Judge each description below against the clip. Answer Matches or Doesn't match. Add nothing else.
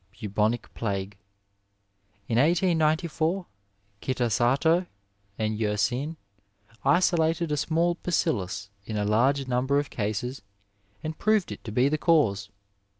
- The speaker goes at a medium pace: Doesn't match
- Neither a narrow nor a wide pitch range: Doesn't match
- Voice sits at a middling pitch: Doesn't match